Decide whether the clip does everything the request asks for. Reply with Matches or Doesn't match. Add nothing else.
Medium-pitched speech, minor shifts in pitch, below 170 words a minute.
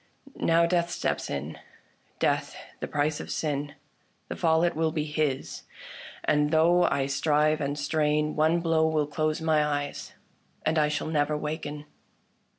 Matches